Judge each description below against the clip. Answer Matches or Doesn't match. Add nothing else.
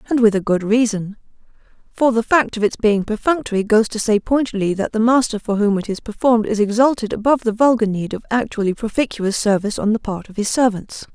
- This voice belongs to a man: Doesn't match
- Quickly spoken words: Matches